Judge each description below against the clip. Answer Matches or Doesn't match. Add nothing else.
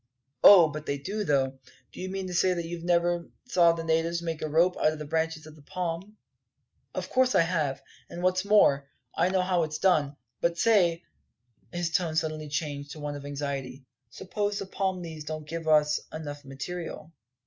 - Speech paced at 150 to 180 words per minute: Doesn't match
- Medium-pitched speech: Matches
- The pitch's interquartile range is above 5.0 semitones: Doesn't match